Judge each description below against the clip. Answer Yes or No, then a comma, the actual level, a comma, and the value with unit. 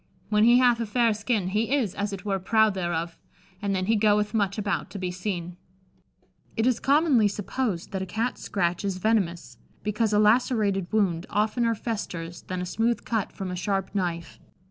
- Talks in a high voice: Yes, high, 205 Hz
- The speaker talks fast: No, average, 190 wpm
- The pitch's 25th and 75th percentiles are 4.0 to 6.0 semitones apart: No, average, 3.4 semitones